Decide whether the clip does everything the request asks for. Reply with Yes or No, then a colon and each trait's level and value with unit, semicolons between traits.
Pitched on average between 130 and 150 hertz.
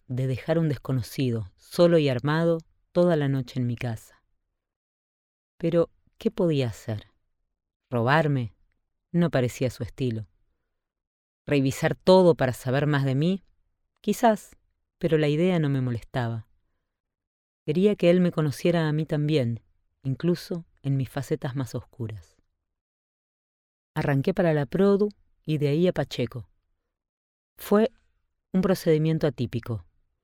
Yes: low, 135 Hz